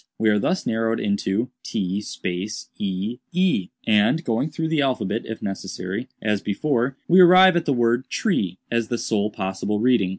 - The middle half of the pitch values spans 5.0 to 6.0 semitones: Yes, average, 5.3 semitones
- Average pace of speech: Yes, average, 160 wpm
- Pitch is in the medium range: No, low, 115 Hz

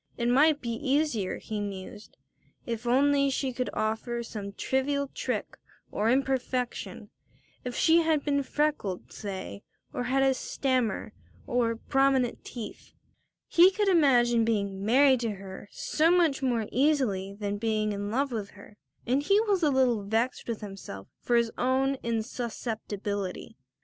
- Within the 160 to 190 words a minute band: No, average, 150 wpm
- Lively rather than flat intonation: No, average, 4.4 semitones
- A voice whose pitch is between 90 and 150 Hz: No, high, 240 Hz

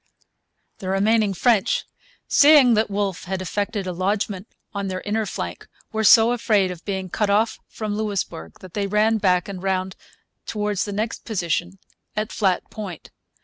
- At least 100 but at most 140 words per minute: No, average, 160 wpm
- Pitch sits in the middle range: No, high, 200 Hz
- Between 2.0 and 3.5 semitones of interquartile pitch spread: Yes, narrow, 2.5 semitones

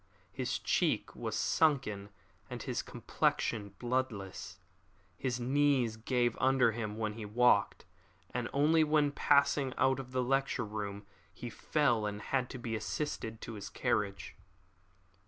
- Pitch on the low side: Yes, low, 120 Hz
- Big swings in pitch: No, average, 3.9 semitones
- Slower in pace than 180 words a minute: Yes, slow, 135 wpm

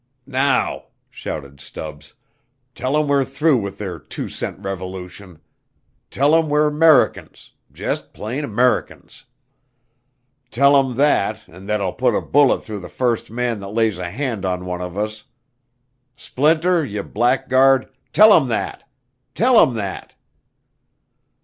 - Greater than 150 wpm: No, slow, 135 wpm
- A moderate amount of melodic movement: No, wide, 6.4 semitones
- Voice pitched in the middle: No, low, 120 Hz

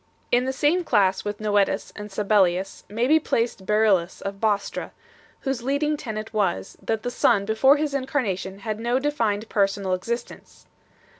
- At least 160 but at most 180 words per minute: Yes, average, 165 wpm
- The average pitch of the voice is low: No, high, 215 Hz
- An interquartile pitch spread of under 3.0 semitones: No, average, 4.5 semitones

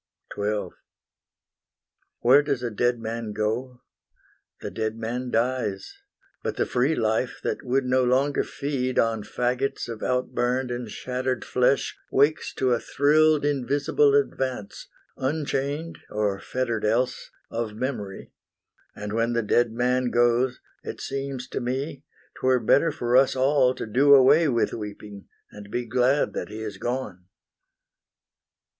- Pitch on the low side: Yes, low, 125 Hz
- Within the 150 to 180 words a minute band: No, average, 140 wpm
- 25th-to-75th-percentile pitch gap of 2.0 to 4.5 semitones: Yes, average, 2.9 semitones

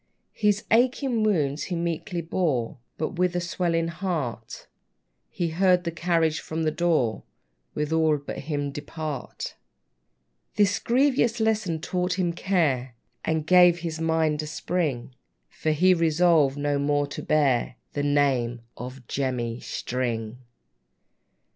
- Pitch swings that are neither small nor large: Yes, average, 3.9 semitones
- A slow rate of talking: Yes, slow, 130 wpm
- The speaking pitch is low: No, medium, 160 Hz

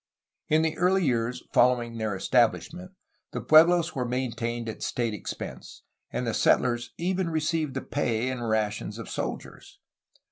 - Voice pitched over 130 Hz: No, low, 125 Hz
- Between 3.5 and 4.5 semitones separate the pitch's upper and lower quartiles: No, wide, 5.4 semitones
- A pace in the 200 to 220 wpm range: No, average, 145 wpm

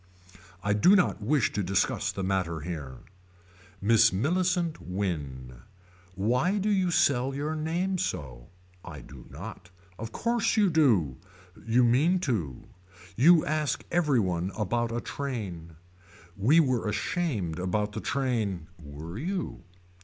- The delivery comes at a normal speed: No, slow, 130 wpm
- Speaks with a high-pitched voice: No, low, 115 Hz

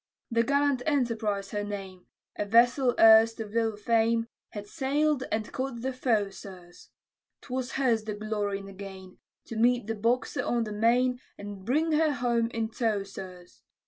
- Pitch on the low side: No, high, 225 Hz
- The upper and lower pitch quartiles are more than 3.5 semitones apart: No, average, 3.2 semitones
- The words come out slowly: No, average, 170 wpm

